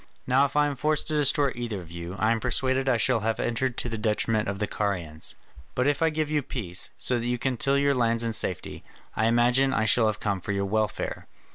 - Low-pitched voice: Yes, low, 120 Hz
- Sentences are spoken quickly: Yes, fast, 245 wpm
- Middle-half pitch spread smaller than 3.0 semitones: No, average, 3.9 semitones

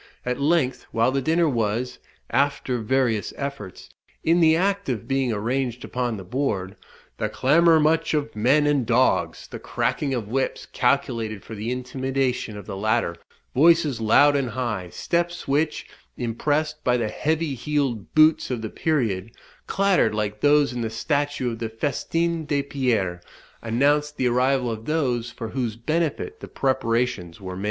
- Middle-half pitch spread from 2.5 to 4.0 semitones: No, average, 4.6 semitones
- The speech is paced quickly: No, average, 160 wpm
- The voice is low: Yes, low, 130 Hz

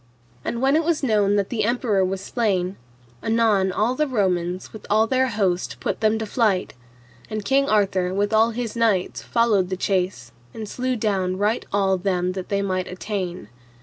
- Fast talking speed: No, average, 180 wpm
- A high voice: Yes, high, 205 Hz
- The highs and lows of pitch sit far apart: No, average, 3.5 semitones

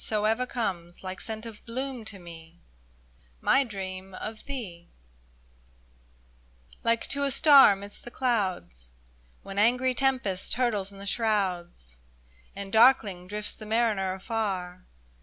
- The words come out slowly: Yes, slow, 130 wpm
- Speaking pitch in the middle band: No, high, 210 Hz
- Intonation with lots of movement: No, average, 4.1 semitones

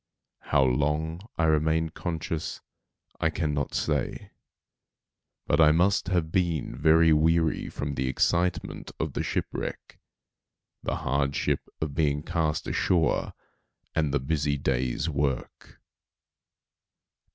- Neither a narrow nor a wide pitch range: No, narrow, 2.3 semitones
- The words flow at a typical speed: No, slow, 115 wpm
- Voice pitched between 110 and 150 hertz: No, very low, 80 Hz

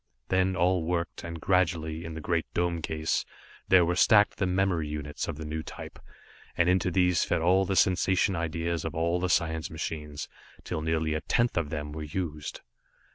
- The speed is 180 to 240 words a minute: Yes, average, 185 wpm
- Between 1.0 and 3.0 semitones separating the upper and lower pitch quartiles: Yes, narrow, 2.5 semitones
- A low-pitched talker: Yes, very low, 85 Hz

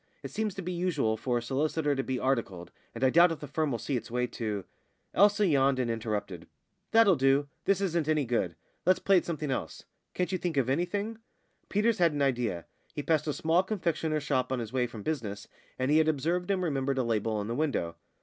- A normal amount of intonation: No, wide, 6.1 semitones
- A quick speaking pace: Yes, fast, 225 wpm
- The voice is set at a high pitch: No, medium, 140 Hz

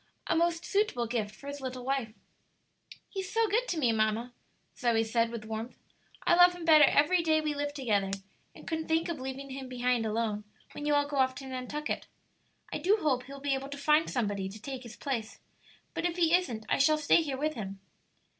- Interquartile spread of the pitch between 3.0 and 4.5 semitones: No, average, 4.9 semitones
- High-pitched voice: Yes, very high, 275 Hz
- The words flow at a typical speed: No, fast, 210 wpm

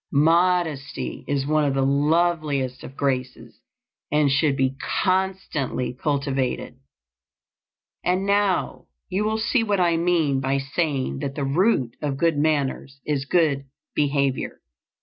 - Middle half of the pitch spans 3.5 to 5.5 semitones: Yes, average, 4.1 semitones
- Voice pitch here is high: No, medium, 145 Hz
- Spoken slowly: Yes, slow, 130 wpm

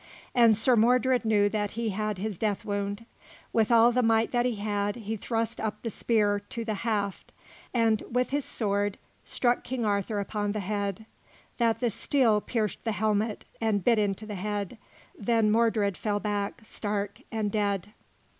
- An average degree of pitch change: No, narrow, 2.0 semitones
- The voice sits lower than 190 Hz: No, high, 215 Hz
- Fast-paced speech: No, average, 175 wpm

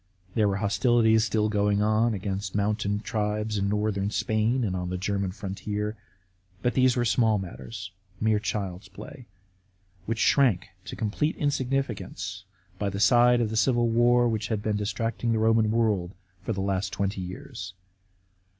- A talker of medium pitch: No, low, 105 Hz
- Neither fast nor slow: Yes, average, 160 wpm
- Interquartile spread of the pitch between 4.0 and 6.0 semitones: No, narrow, 2.5 semitones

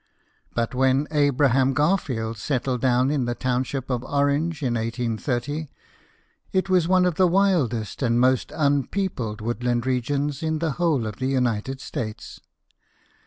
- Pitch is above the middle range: No, low, 130 Hz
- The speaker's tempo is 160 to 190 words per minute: No, average, 145 wpm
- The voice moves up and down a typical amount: Yes, average, 3.7 semitones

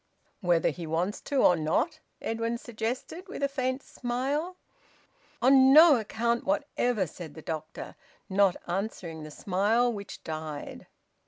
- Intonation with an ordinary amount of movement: No, wide, 7.1 semitones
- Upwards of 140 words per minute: No, slow, 135 wpm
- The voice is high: Yes, high, 225 Hz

